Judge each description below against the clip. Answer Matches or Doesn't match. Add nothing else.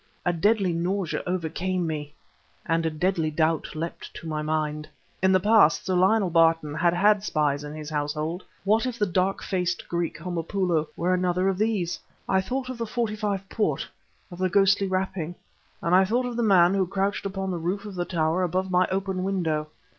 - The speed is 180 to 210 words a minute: Matches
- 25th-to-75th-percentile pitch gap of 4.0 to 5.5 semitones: Doesn't match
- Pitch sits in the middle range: Matches